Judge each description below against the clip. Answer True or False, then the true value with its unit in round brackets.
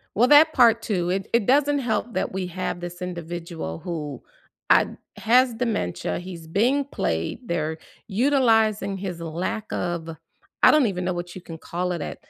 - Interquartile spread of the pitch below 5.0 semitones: False (5.4 semitones)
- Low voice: False (185 Hz)